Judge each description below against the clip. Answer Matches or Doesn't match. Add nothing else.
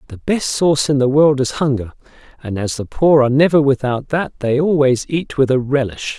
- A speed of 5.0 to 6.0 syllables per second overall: Matches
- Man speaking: Matches